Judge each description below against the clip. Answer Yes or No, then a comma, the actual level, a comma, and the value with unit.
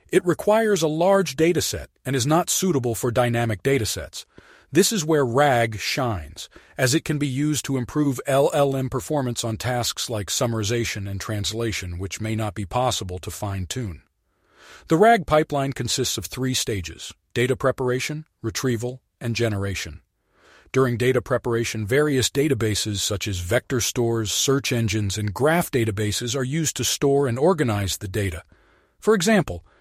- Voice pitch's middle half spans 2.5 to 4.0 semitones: No, average, 4.7 semitones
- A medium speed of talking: Yes, average, 155 wpm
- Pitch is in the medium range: No, low, 125 Hz